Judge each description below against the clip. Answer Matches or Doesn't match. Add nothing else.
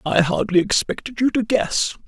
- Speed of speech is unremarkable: Matches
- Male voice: Matches